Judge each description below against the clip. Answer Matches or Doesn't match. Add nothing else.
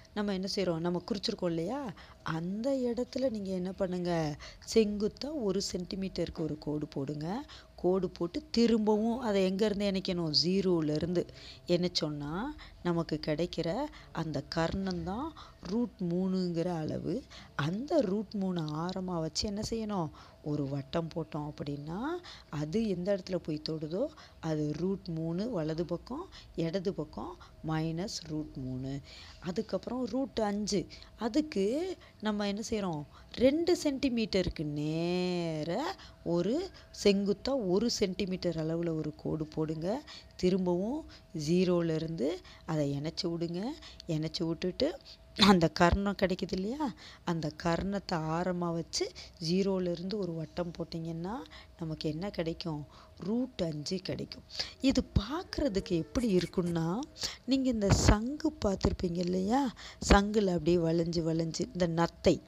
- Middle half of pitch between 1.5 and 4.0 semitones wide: Doesn't match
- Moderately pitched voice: Matches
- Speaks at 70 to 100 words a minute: Doesn't match